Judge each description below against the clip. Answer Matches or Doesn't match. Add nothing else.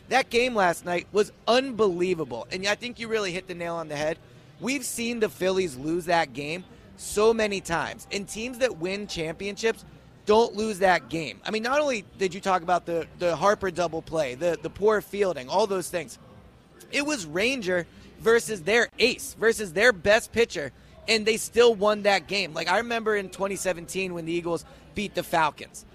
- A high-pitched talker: Matches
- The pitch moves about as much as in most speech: Matches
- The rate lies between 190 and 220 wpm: Matches